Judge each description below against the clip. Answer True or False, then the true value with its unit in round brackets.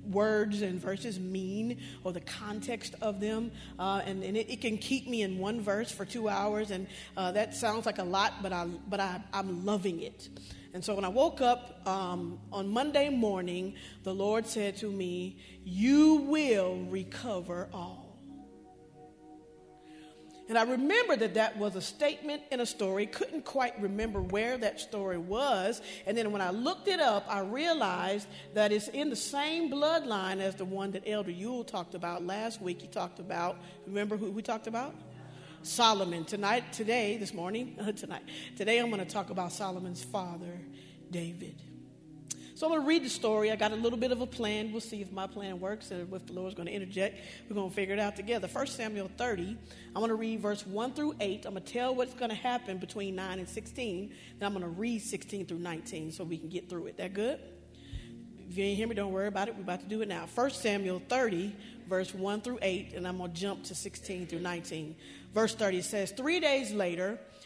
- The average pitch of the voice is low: False (200 Hz)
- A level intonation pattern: False (3.5 semitones)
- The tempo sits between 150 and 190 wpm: False (205 wpm)